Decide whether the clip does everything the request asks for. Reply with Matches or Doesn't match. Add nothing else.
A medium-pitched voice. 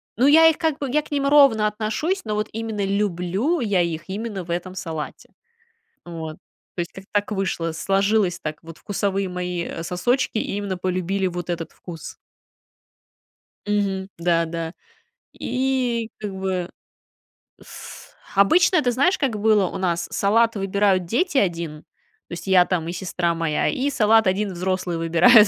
Doesn't match